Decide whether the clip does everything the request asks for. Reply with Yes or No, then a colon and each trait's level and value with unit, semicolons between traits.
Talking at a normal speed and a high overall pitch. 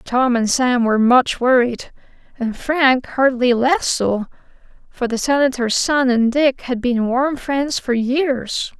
Yes: average, 155 wpm; very high, 255 Hz